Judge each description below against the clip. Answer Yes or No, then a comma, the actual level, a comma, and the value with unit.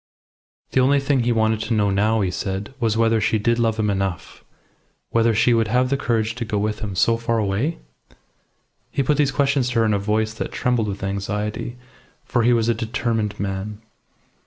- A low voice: Yes, low, 110 Hz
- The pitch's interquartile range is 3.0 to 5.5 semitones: No, narrow, 2.4 semitones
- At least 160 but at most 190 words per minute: No, fast, 205 wpm